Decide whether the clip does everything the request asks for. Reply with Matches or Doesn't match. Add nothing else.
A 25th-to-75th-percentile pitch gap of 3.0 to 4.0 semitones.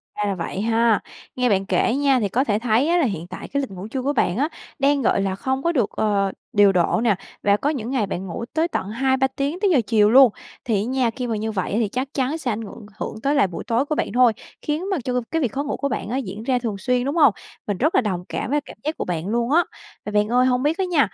Doesn't match